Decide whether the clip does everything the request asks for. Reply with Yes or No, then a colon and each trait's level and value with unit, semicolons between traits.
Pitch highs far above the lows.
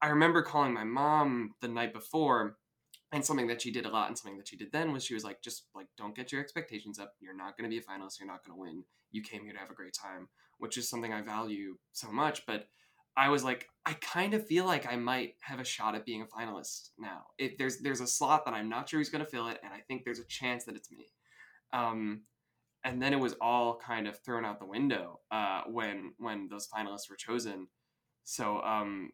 No: average, 3.8 semitones